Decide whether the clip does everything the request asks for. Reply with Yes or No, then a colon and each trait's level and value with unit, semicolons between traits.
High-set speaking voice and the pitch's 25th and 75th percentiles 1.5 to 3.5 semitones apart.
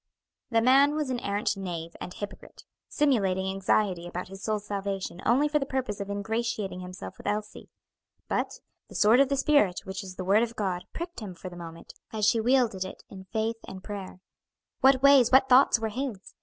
No: high, 210 Hz; average, 5.0 semitones